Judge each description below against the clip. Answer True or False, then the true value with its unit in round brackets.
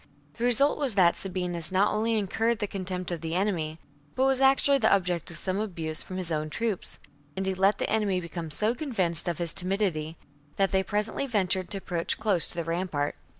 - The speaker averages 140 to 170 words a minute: False (205 wpm)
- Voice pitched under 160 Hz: False (190 Hz)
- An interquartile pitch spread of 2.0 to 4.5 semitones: True (3.8 semitones)